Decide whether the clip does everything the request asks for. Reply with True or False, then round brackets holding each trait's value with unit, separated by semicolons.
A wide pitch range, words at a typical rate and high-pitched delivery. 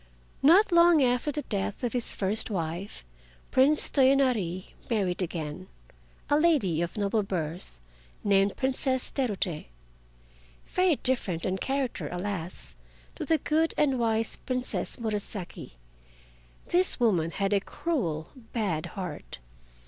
False (6.6 semitones; 120 wpm; 220 Hz)